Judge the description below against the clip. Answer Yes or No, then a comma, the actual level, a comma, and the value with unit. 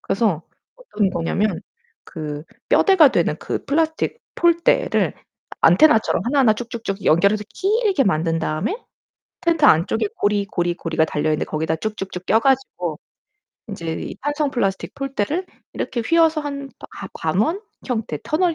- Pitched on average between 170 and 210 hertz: No, high, 220 Hz